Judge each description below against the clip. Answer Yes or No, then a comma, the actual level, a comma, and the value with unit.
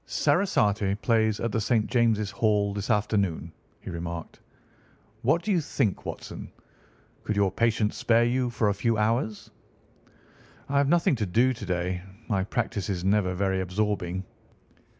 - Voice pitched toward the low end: Yes, low, 105 Hz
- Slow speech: No, average, 150 wpm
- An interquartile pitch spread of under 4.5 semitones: Yes, average, 3.4 semitones